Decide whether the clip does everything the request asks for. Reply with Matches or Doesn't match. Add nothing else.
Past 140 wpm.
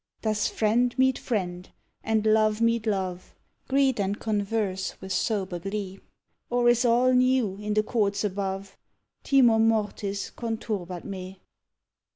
Doesn't match